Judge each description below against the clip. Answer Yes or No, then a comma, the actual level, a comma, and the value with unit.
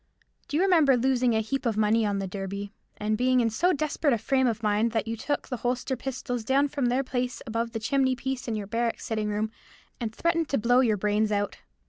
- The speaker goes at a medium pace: No, fast, 230 wpm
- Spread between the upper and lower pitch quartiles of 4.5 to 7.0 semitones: No, average, 3.6 semitones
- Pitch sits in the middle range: No, high, 235 Hz